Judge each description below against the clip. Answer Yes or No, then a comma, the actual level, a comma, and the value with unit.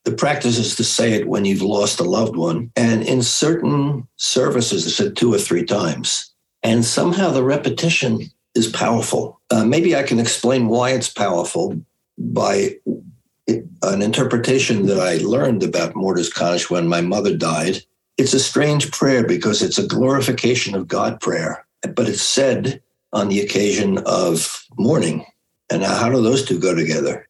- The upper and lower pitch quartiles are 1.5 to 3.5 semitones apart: No, average, 4.3 semitones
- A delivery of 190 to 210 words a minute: No, average, 165 wpm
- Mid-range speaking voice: No, low, 120 Hz